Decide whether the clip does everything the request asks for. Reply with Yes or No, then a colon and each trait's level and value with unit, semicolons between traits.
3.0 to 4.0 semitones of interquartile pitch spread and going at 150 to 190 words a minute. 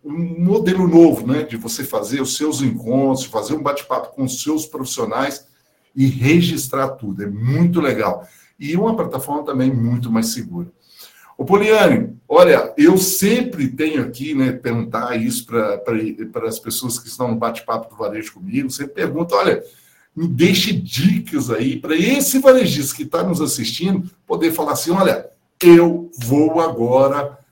No: average, 4.9 semitones; average, 155 wpm